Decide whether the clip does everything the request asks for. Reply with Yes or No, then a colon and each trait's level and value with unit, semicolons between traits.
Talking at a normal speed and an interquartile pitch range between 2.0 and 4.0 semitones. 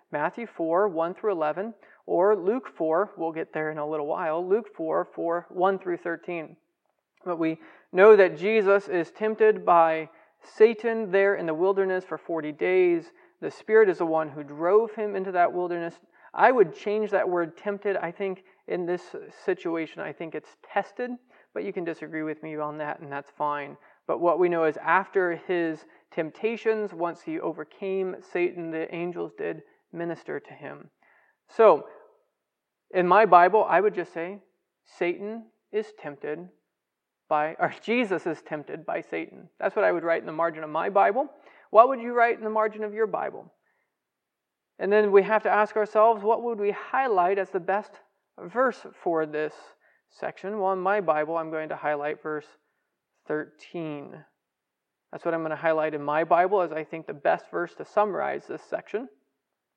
No: average, 180 wpm; average, 4.7 semitones